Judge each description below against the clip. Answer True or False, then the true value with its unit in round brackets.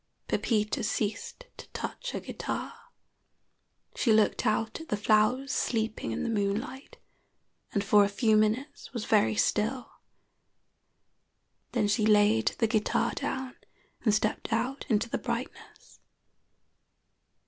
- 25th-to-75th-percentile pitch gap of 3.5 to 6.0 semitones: False (2.9 semitones)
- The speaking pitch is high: True (220 Hz)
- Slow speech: True (125 wpm)